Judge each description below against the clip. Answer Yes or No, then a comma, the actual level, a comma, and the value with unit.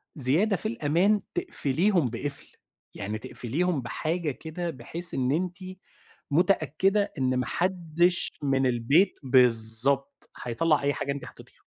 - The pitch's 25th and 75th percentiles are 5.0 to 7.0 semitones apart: Yes, wide, 5.5 semitones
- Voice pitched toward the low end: No, medium, 150 Hz